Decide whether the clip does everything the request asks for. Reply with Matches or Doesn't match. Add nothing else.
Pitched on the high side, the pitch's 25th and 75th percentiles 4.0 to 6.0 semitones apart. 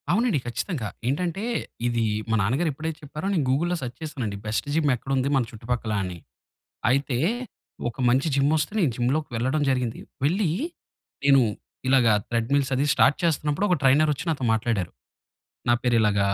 Doesn't match